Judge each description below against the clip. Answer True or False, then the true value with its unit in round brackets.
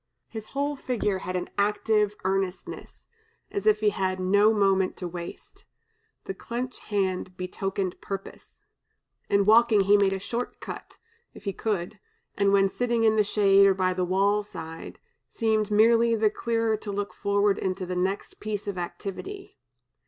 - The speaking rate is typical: True (160 wpm)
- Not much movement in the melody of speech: True (2.3 semitones)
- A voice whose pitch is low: False (200 Hz)